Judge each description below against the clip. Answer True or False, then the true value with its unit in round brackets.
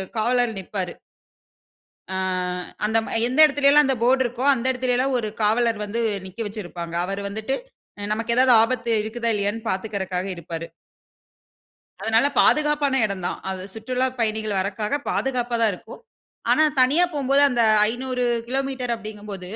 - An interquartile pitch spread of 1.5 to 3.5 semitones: False (3.9 semitones)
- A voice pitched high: True (230 Hz)